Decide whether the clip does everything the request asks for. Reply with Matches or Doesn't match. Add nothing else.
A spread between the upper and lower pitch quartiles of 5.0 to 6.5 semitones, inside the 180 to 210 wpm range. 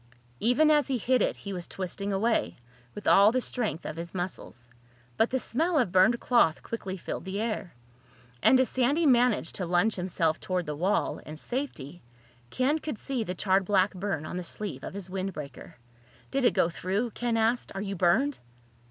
Matches